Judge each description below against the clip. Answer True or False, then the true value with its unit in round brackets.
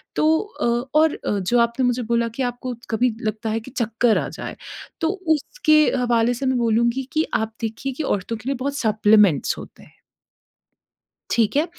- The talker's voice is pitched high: True (235 Hz)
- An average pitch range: True (3.2 semitones)